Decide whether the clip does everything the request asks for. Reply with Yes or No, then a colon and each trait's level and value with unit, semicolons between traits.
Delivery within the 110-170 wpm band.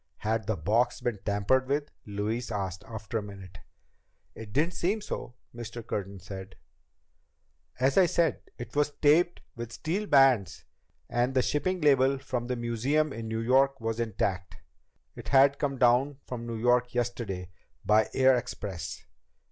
Yes: average, 155 wpm